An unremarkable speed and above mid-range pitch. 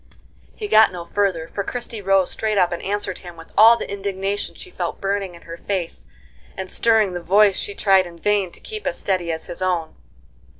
No: fast, 210 wpm; high, 195 Hz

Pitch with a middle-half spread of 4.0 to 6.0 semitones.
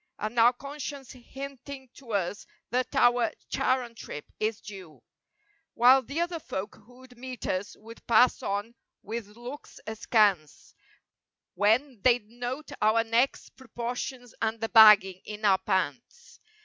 No: average, 3.3 semitones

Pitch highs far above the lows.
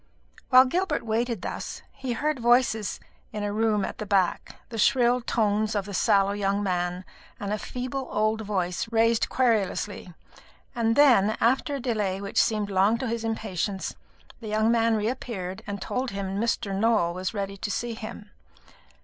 No: average, 2.9 semitones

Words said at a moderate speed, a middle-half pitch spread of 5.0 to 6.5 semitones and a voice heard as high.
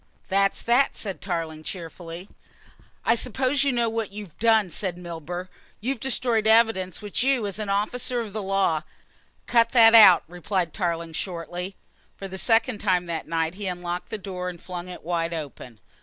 No: average, 175 wpm; average, 4.4 semitones; high, 195 Hz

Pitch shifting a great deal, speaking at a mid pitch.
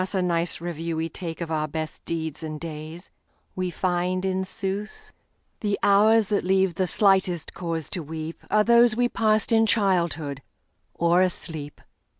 No: average, 3.5 semitones; medium, 180 Hz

